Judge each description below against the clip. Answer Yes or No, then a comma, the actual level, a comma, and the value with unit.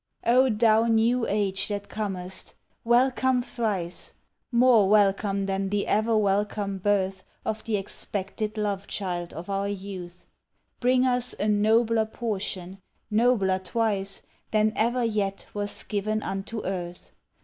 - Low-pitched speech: No, high, 210 Hz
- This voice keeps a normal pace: No, slow, 125 wpm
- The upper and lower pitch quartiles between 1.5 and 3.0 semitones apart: Yes, average, 2.7 semitones